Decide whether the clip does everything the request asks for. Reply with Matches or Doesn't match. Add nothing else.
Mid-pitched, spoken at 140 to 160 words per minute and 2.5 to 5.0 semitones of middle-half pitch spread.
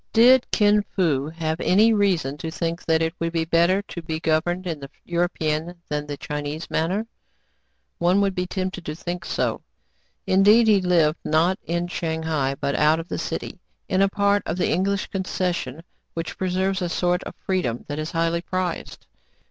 Doesn't match